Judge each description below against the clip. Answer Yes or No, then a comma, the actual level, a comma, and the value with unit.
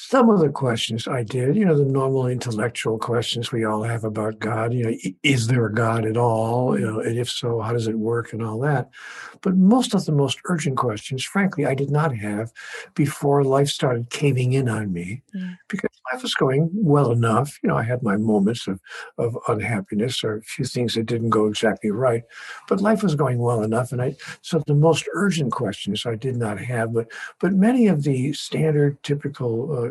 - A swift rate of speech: Yes, fast, 210 wpm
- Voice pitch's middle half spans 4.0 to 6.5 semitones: Yes, average, 4.3 semitones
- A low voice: Yes, low, 125 Hz